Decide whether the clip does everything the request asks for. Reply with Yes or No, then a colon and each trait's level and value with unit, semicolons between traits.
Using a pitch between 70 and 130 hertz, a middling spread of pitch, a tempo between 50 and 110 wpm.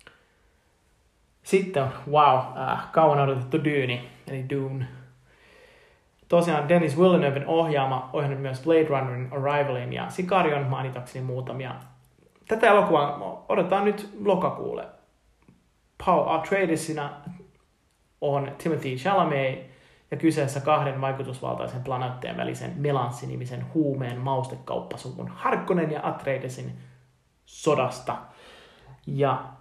No: medium, 140 Hz; average, 3.8 semitones; slow, 95 wpm